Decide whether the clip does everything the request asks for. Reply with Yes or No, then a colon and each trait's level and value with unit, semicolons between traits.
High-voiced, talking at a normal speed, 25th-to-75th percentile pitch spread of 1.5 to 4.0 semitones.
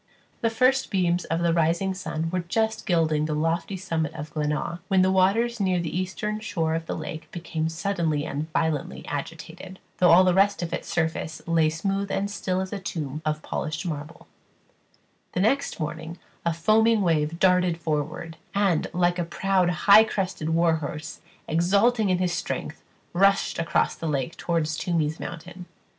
No: medium, 170 Hz; average, 170 wpm; average, 3.1 semitones